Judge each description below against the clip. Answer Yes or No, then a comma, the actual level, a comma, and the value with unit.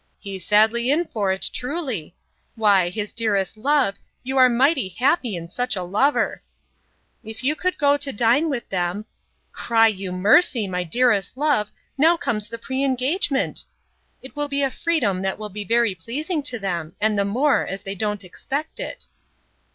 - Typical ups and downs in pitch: No, wide, 5.8 semitones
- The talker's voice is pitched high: Yes, high, 230 Hz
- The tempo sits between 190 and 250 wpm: No, average, 160 wpm